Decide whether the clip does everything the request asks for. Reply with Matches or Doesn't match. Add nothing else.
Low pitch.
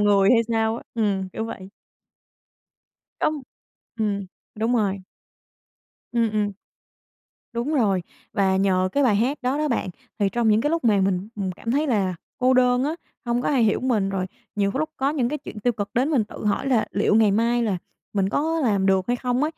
Doesn't match